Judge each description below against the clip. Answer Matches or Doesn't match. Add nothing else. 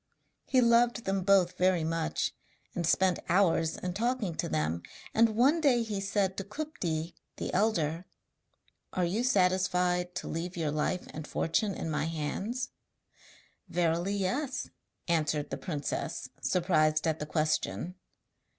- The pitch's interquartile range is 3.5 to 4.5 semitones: Matches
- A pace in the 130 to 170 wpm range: Matches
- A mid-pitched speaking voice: Matches